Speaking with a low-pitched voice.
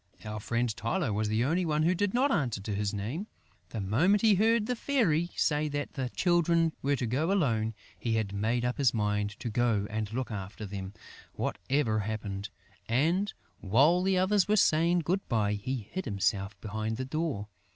Yes: low, 125 Hz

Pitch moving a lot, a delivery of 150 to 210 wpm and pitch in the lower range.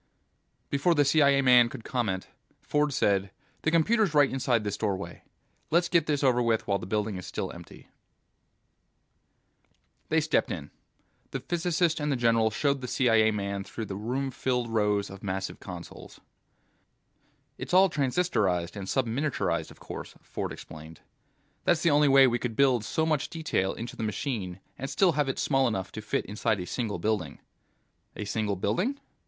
Yes: wide, 5.9 semitones; average, 170 wpm; low, 120 Hz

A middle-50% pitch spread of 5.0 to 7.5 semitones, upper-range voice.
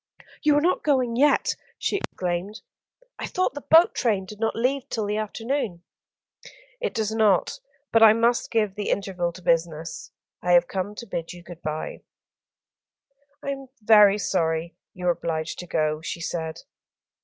Yes: wide, 5.4 semitones; high, 205 Hz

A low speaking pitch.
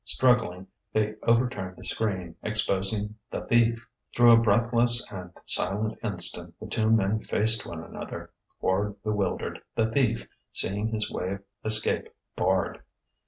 Yes: low, 110 Hz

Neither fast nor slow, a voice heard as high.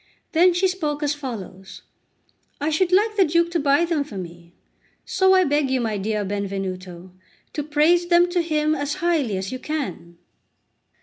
Yes: average, 175 wpm; very high, 295 Hz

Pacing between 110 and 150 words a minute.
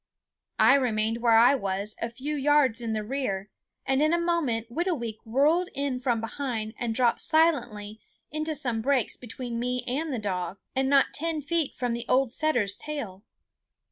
No: average, 170 wpm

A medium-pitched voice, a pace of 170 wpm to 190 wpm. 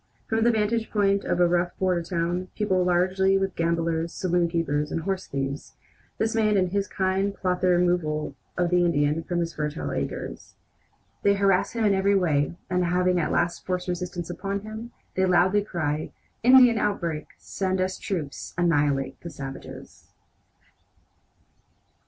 No: medium, 180 Hz; average, 155 wpm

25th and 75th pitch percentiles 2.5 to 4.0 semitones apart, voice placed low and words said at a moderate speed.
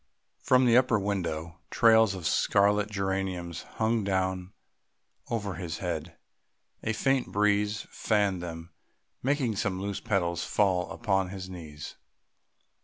No: average, 3.1 semitones; very low, 95 Hz; slow, 120 wpm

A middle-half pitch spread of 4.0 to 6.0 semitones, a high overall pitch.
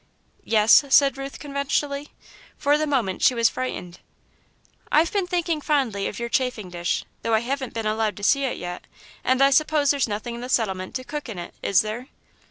Yes: average, 4.7 semitones; very high, 255 Hz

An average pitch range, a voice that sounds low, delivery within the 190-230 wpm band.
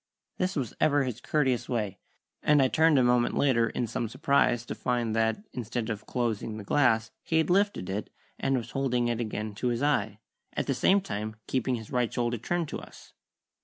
Yes: average, 3.8 semitones; low, 120 Hz; average, 200 wpm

